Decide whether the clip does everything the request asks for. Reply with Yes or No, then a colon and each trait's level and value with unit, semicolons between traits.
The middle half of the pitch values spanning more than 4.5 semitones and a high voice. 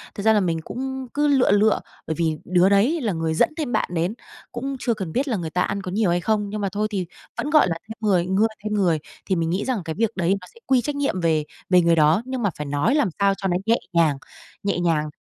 Yes: average, 5.3 semitones; high, 195 Hz